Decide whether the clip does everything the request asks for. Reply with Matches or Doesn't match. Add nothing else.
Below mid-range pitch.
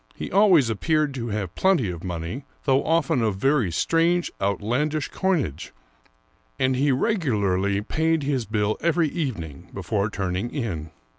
Matches